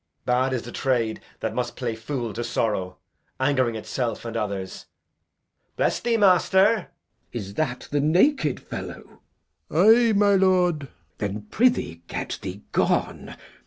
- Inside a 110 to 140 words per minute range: No, average, 150 wpm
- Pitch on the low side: Yes, low, 130 Hz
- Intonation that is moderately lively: No, wide, 8.6 semitones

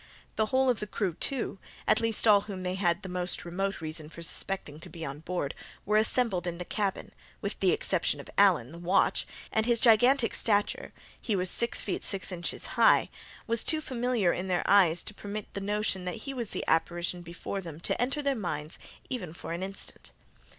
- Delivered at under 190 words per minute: No, average, 200 wpm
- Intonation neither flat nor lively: Yes, average, 4.1 semitones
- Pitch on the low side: No, high, 195 Hz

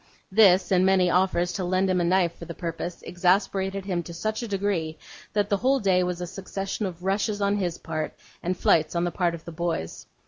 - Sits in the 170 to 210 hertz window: Yes, medium, 185 Hz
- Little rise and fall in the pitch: Yes, narrow, 2.2 semitones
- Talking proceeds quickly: Yes, fast, 220 wpm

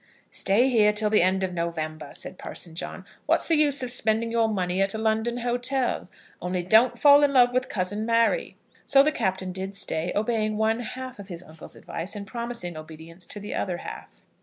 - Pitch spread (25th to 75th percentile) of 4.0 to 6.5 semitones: Yes, average, 4.9 semitones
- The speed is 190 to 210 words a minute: Yes, average, 200 wpm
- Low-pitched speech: No, high, 215 Hz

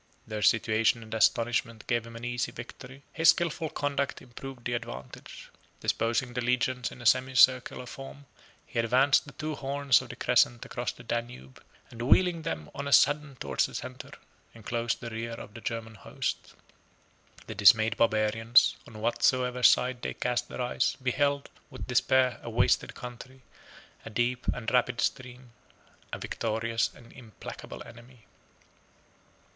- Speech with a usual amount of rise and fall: No, narrow, 2.1 semitones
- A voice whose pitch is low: Yes, low, 120 Hz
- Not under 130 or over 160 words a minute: Yes, average, 150 wpm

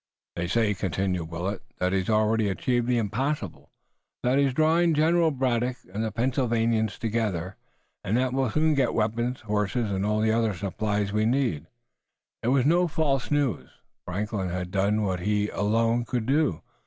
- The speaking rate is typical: Yes, average, 165 wpm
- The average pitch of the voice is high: No, low, 110 Hz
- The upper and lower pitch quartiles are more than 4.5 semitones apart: No, average, 4.2 semitones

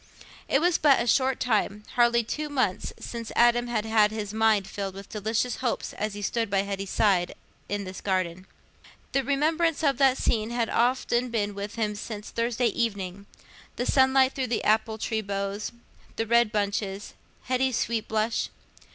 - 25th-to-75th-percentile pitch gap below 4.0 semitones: Yes, average, 3.2 semitones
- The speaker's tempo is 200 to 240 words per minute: No, average, 165 wpm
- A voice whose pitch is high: Yes, high, 220 Hz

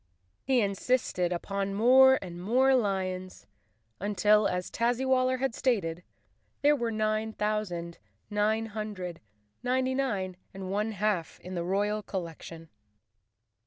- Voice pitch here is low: No, high, 210 Hz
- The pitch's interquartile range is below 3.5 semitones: No, average, 4.4 semitones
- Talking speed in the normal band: No, slow, 125 wpm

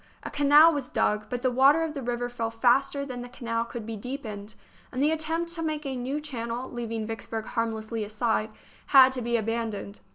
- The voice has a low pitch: No, high, 245 Hz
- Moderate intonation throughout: Yes, average, 3.6 semitones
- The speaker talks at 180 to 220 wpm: Yes, average, 200 wpm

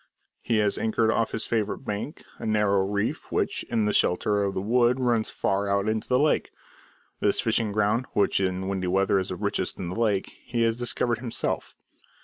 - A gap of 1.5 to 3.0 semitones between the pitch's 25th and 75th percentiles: Yes, average, 2.7 semitones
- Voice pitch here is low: Yes, low, 105 Hz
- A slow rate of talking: No, average, 195 wpm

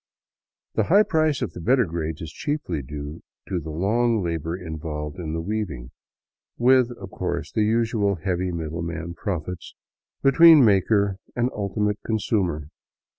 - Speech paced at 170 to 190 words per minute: No, average, 145 wpm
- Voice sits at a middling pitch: No, very low, 95 Hz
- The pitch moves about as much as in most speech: No, wide, 5.8 semitones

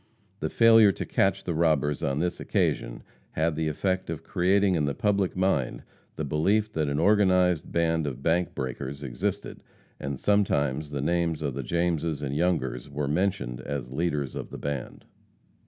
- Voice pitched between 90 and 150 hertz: No, very low, 80 Hz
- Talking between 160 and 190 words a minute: Yes, average, 170 wpm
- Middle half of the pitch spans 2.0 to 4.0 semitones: No, average, 4.4 semitones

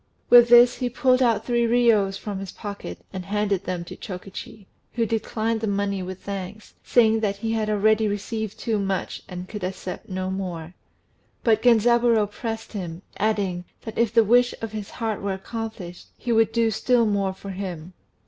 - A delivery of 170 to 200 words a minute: Yes, average, 180 wpm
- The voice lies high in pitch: Yes, high, 210 Hz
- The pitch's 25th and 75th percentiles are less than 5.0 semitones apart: Yes, average, 2.8 semitones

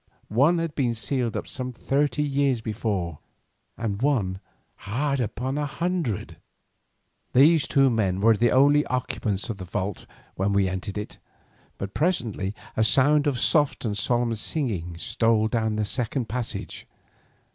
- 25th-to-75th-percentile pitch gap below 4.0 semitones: No, average, 5.2 semitones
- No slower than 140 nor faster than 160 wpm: Yes, average, 145 wpm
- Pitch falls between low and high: No, low, 120 Hz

